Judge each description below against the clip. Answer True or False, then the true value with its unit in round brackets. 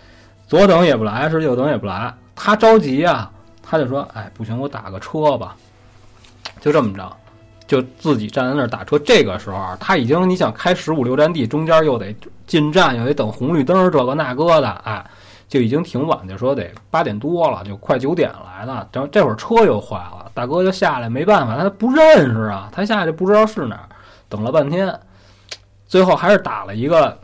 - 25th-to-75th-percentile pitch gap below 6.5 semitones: False (7.3 semitones)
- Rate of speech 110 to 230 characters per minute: False (295 characters per minute)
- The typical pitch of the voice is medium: False (125 Hz)